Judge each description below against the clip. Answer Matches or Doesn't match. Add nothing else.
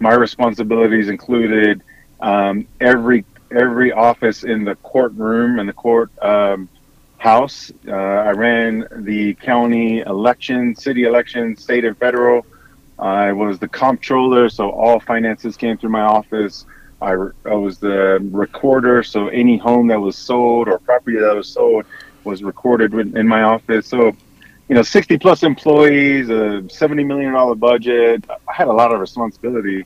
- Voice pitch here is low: Matches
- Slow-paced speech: Doesn't match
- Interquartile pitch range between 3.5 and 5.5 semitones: Doesn't match